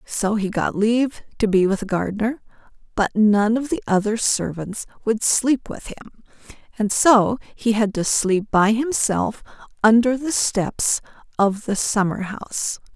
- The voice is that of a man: No, female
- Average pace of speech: Yes, average, 155 wpm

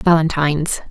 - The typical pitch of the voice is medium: Yes, medium, 155 Hz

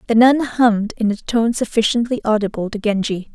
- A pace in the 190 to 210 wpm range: No, average, 180 wpm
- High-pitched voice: Yes, high, 225 Hz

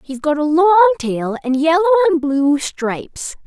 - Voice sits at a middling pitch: No, very high, 315 Hz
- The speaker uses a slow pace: No, average, 175 wpm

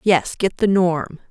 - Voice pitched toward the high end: No, medium, 180 Hz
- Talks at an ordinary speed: Yes, average, 185 wpm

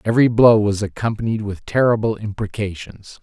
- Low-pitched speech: Yes, low, 105 Hz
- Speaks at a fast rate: No, slow, 130 wpm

